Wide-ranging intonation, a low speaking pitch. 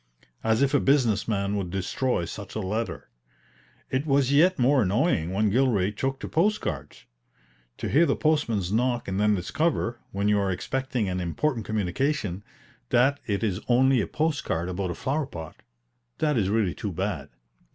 Yes: wide, 5.8 semitones; low, 110 Hz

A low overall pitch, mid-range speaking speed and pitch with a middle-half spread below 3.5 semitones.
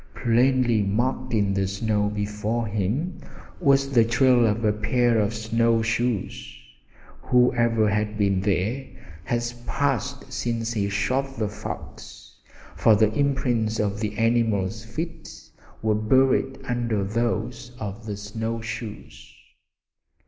No: low, 115 Hz; slow, 125 wpm; average, 2.8 semitones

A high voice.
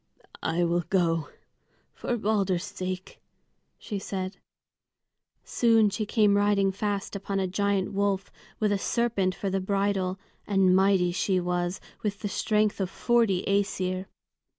Yes: high, 195 Hz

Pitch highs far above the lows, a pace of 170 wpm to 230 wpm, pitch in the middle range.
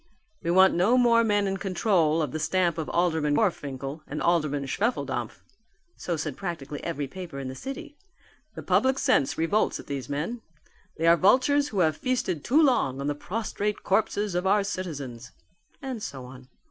Yes: wide, 6.4 semitones; average, 175 wpm; medium, 175 Hz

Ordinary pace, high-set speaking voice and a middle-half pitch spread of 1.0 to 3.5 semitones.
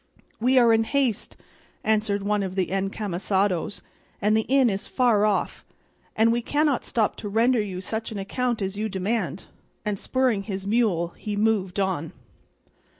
Yes: average, 160 wpm; high, 210 Hz; average, 2.9 semitones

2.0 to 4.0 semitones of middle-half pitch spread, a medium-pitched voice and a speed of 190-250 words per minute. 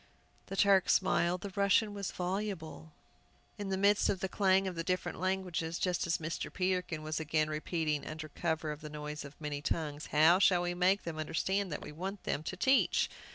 Yes: average, 3.5 semitones; medium, 175 Hz; average, 200 wpm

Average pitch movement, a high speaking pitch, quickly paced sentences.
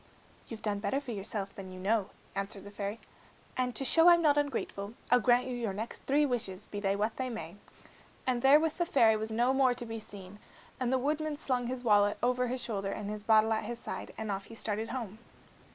Yes: average, 3.9 semitones; high, 225 Hz; fast, 225 wpm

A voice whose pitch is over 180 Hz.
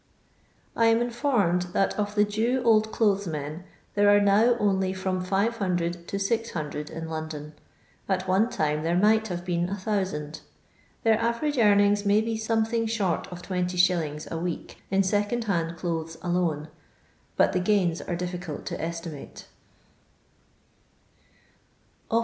Yes: high, 190 Hz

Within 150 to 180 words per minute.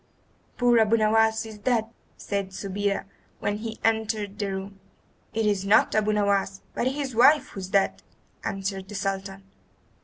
Yes: average, 155 wpm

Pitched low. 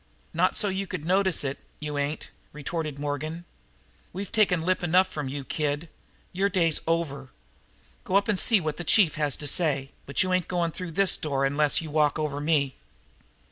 No: medium, 160 Hz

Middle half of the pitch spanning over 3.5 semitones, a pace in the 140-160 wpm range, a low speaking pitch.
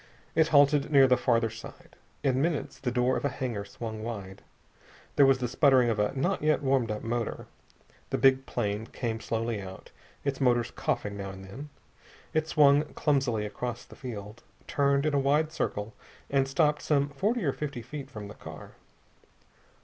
No: average, 4.0 semitones; average, 180 wpm; low, 130 Hz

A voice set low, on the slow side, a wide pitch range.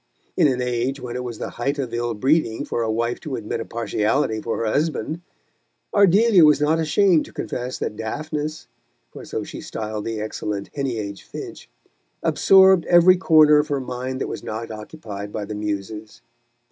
No: low, 125 Hz; average, 180 wpm; wide, 5.8 semitones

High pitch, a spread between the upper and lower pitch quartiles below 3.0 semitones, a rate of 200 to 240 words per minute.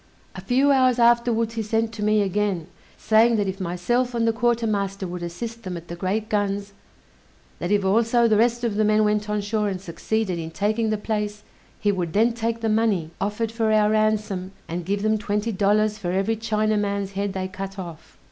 Yes: high, 210 Hz; narrow, 2.5 semitones; fast, 205 wpm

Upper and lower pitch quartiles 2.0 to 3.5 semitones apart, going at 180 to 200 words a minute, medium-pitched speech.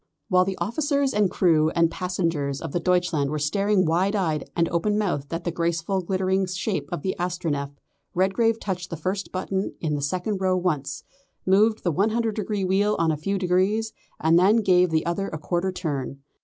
Yes: average, 3.2 semitones; average, 190 wpm; medium, 180 Hz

